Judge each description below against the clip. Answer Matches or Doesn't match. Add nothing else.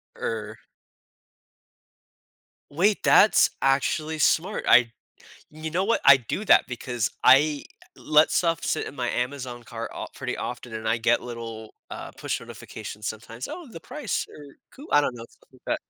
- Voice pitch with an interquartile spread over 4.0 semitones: Matches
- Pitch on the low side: Matches